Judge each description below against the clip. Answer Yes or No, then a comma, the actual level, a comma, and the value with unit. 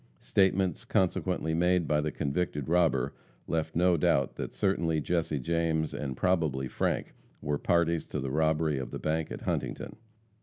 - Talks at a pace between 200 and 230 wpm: No, average, 155 wpm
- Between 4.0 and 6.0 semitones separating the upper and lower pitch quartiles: No, average, 2.8 semitones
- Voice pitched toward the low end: Yes, very low, 80 Hz